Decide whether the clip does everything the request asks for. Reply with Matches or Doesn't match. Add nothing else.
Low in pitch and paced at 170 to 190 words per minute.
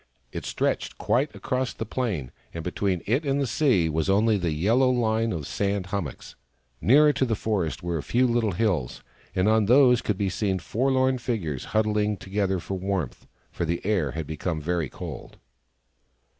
Matches